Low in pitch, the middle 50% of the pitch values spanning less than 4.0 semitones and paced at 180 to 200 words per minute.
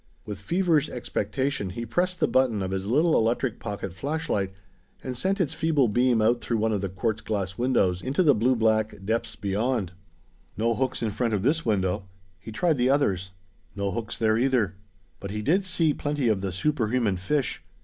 No: low, 115 Hz; average, 5.2 semitones; average, 190 wpm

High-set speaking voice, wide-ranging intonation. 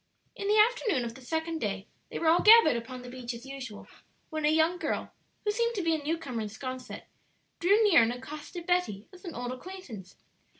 Yes: very high, 305 Hz; wide, 6.6 semitones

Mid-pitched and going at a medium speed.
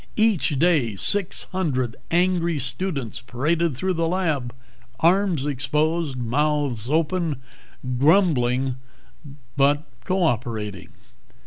No: medium, 150 Hz; slow, 95 wpm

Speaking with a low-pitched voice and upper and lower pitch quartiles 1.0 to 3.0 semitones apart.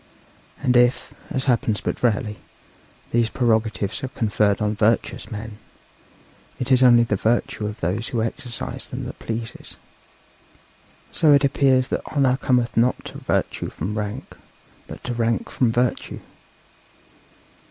Yes: low, 115 Hz; average, 2.7 semitones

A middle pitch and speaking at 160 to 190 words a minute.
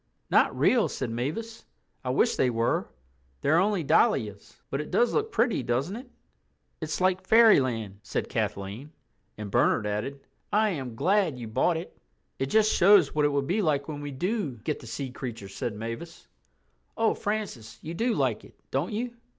Yes: medium, 145 Hz; average, 175 wpm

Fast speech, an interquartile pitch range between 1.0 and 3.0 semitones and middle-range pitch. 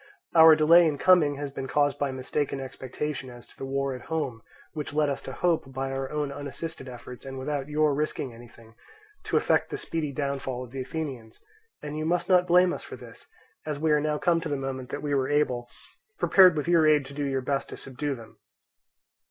Yes: fast, 215 wpm; narrow, 2.6 semitones; medium, 145 Hz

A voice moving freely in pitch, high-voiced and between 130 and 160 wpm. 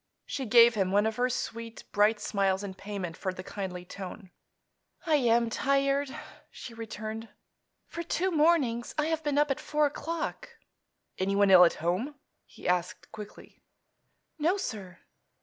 Yes: wide, 6.5 semitones; high, 225 Hz; average, 150 wpm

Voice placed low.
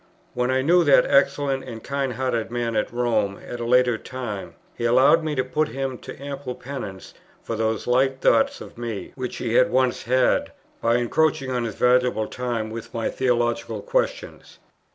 Yes: low, 125 Hz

